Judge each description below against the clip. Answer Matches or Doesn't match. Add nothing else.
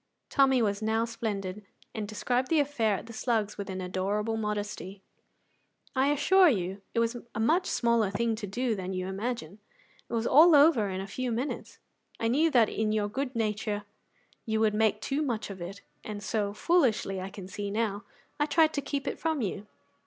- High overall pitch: Matches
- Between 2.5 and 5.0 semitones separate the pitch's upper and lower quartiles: Matches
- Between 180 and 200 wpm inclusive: Matches